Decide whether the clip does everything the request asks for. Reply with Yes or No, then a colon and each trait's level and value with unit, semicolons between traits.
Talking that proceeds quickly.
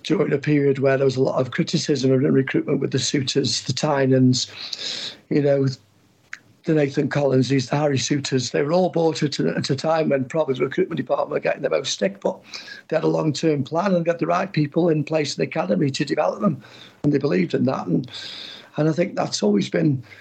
Yes: fast, 220 wpm